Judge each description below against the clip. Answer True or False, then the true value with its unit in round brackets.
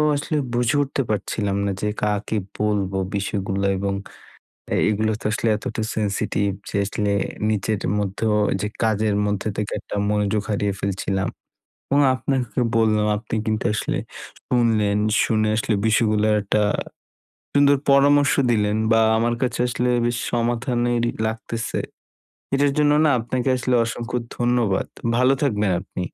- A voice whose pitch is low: True (110 Hz)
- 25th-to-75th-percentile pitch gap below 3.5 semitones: True (2.9 semitones)